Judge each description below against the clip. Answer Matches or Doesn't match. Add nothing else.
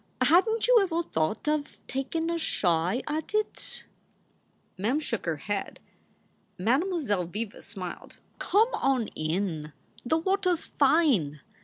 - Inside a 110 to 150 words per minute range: Matches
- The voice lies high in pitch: Matches